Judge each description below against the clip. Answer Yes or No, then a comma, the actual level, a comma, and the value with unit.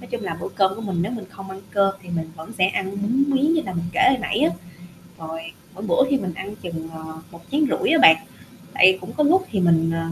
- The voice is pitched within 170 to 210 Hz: Yes, high, 190 Hz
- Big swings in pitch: Yes, wide, 6.2 semitones